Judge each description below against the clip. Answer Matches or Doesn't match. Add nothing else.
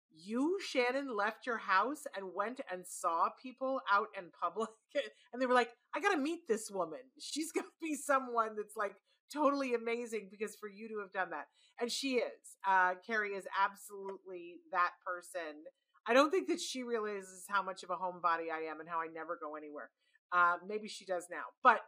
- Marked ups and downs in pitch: Matches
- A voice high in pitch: Matches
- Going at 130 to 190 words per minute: Doesn't match